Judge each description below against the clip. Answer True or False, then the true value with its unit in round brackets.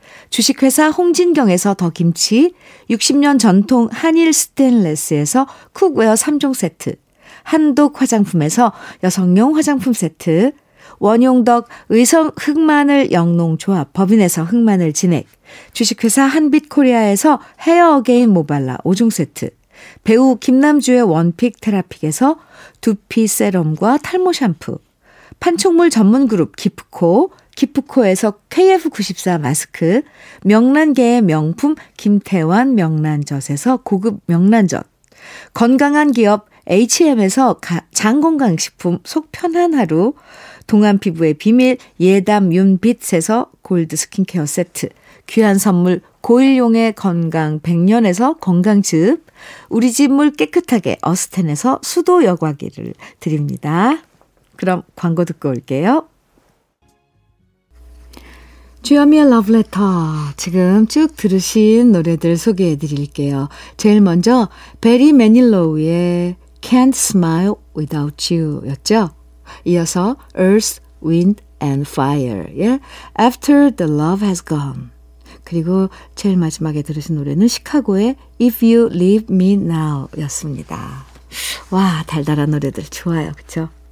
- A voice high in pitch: True (205 Hz)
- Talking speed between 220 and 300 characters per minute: True (275 characters per minute)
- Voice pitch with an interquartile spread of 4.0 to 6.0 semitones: False (7.4 semitones)